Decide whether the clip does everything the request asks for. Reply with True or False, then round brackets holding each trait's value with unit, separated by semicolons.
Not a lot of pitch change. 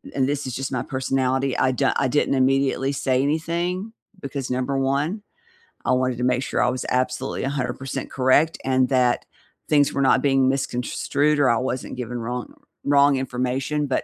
True (1.7 semitones)